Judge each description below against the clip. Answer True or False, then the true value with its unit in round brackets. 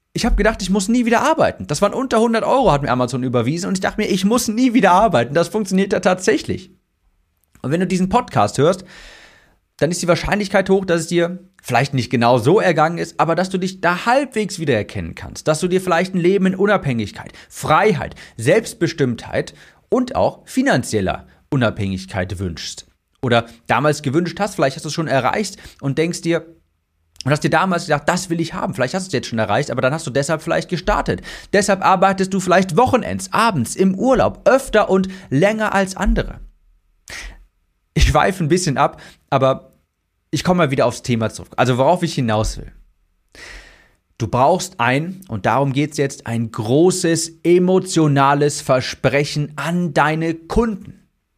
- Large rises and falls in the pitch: True (6.6 semitones)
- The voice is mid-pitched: True (165 Hz)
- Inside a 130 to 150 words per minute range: False (180 wpm)